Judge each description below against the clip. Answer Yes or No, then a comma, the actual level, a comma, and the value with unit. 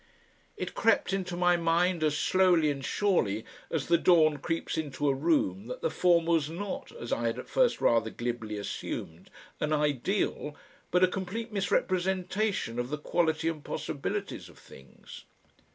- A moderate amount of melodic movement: Yes, average, 4.4 semitones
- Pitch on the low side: No, medium, 165 Hz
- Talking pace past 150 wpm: Yes, average, 160 wpm